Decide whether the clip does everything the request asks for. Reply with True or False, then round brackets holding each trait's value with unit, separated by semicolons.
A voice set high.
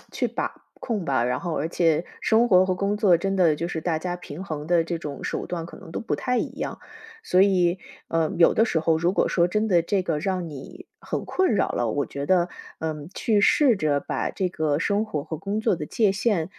False (175 Hz)